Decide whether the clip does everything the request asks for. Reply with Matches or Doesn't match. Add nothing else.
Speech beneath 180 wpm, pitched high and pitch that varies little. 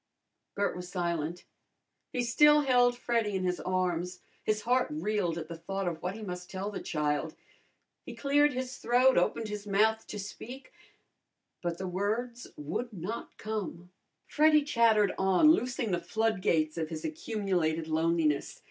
Doesn't match